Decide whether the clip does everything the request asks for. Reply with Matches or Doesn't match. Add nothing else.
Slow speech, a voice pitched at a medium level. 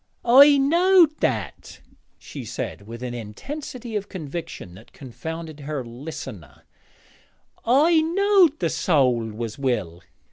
Matches